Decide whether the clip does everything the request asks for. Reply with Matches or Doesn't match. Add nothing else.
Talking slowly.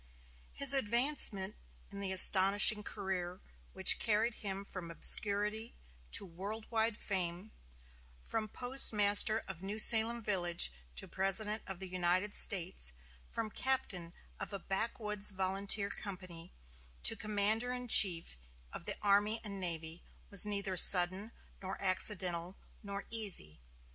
Matches